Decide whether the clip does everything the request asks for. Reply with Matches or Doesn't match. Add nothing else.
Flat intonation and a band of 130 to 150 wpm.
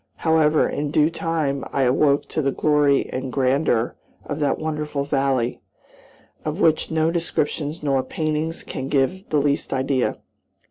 Matches